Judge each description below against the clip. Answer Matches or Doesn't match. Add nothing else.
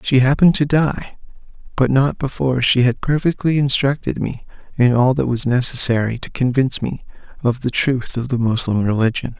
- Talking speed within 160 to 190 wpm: Matches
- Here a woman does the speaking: Doesn't match